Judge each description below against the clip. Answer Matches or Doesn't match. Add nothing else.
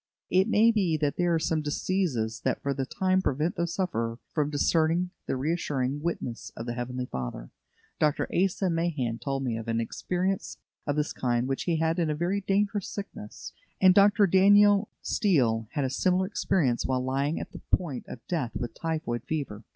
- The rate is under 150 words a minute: Doesn't match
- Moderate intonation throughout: Doesn't match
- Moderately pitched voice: Matches